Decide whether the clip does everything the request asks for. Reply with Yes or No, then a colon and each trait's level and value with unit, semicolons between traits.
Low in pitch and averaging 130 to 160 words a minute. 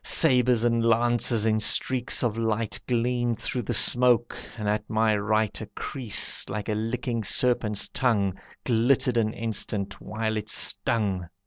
Yes: low, 115 Hz; average, 145 wpm